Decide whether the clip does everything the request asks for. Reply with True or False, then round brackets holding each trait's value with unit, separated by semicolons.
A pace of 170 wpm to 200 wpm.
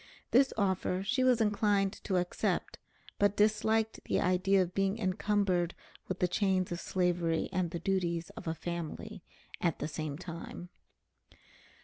False (145 wpm)